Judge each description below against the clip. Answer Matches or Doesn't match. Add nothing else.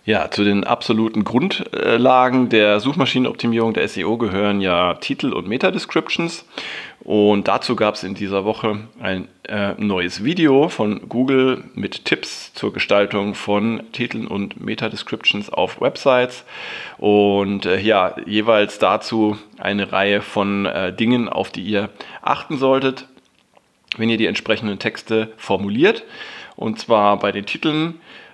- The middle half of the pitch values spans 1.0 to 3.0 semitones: Matches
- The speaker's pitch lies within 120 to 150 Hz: Doesn't match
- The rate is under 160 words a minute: Matches